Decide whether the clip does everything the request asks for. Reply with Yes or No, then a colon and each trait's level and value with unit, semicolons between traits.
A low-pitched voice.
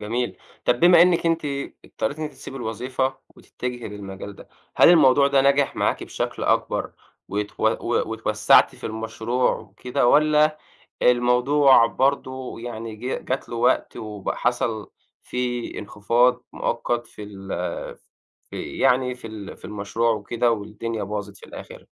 Yes: low, 120 Hz